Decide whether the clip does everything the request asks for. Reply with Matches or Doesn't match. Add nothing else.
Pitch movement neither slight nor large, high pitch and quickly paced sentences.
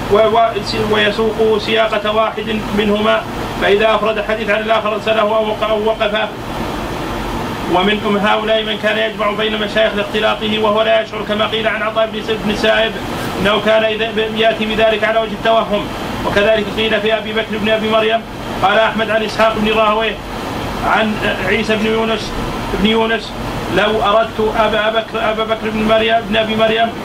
Doesn't match